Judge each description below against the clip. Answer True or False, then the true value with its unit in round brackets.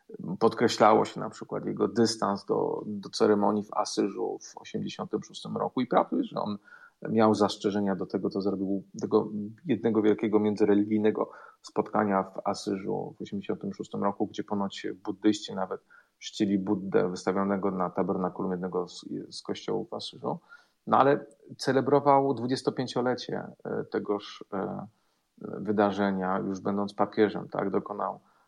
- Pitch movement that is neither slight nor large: False (2.0 semitones)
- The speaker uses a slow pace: False (130 wpm)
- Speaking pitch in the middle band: False (105 Hz)